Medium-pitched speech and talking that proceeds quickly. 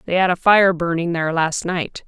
Yes: medium, 175 Hz; fast, 230 wpm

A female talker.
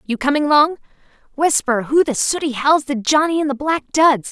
Yes: female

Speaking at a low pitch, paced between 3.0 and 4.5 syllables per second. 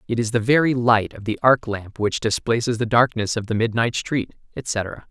No: low, 115 Hz; 4.8 syllables/s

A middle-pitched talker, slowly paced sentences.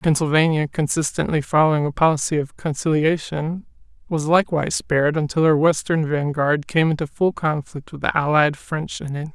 No: medium, 155 Hz; average, 155 wpm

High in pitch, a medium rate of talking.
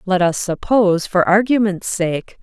Yes: high, 195 Hz; average, 150 wpm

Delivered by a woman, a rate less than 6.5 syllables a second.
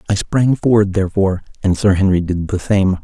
No: male; 5.7 syllables/s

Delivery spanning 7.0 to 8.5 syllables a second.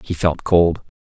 No: 4.1 syllables/s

